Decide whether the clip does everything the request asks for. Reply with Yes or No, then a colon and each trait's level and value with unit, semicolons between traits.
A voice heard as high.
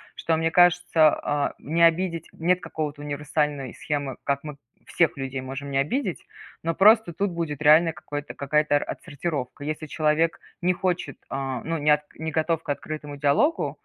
No: medium, 155 Hz